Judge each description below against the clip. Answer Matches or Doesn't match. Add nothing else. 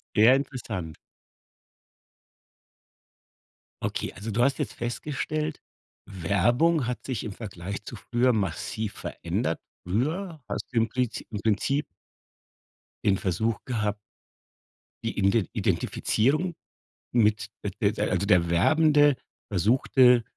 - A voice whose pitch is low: Matches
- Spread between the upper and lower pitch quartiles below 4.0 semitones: Doesn't match